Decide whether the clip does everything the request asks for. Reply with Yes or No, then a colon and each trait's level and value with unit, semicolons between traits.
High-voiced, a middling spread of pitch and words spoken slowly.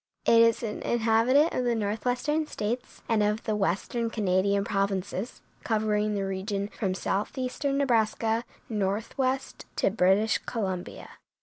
Yes: high, 220 Hz; average, 3.1 semitones; slow, 125 wpm